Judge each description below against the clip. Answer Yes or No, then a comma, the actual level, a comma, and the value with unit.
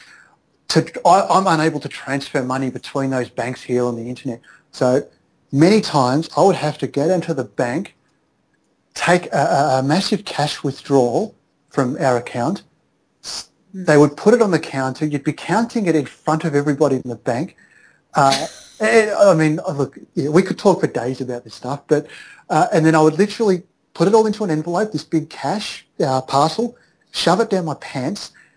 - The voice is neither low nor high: Yes, medium, 155 Hz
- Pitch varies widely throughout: No, average, 4.9 semitones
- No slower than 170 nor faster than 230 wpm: Yes, average, 185 wpm